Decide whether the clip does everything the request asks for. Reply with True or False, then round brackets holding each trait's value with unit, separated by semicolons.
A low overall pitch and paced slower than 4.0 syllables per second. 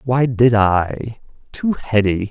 True (115 Hz; 3.2 syllables/s)